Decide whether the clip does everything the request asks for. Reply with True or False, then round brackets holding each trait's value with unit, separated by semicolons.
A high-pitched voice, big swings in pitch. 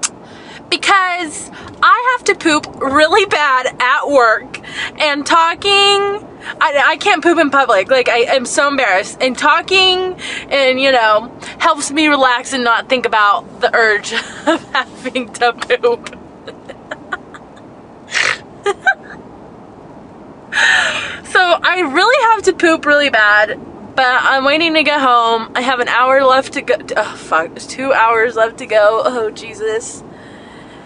True (285 Hz; 6.5 semitones)